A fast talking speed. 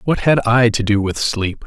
Yes: fast, 255 wpm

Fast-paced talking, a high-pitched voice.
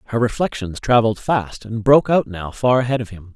No: fast, 215 wpm; low, 115 Hz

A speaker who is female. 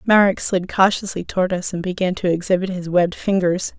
Yes: female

